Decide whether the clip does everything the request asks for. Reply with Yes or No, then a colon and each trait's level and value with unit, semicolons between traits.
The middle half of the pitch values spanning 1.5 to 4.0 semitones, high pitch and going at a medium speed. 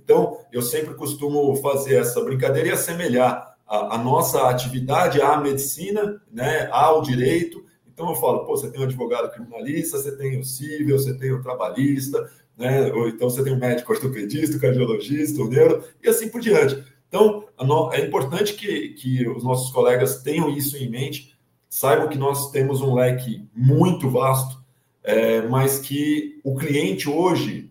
No: average, 2.9 semitones; low, 135 Hz; average, 165 wpm